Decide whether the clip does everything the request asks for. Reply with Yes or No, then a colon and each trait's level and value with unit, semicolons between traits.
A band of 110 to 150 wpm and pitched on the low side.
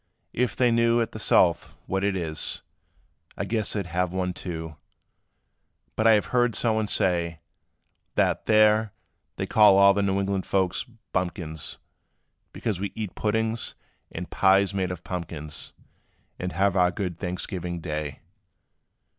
Yes: average, 145 wpm; very low, 95 Hz